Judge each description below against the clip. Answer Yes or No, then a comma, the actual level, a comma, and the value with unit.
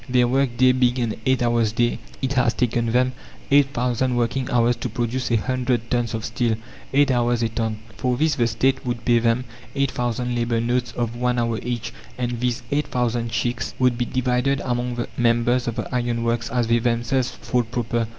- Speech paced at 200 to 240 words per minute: Yes, fast, 205 wpm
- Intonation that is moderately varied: No, narrow, 1.3 semitones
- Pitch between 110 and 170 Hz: Yes, low, 120 Hz